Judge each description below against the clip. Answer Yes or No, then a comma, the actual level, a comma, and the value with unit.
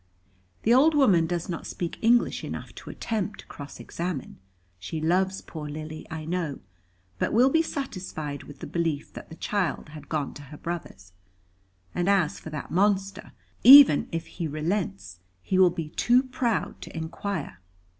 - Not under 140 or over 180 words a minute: Yes, average, 165 wpm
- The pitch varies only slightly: No, average, 4.7 semitones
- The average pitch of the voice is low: No, medium, 170 Hz